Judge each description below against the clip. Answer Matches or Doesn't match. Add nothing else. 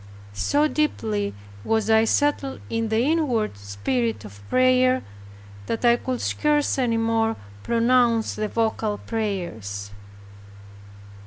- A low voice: Doesn't match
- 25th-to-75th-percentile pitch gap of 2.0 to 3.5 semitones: Doesn't match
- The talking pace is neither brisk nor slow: Doesn't match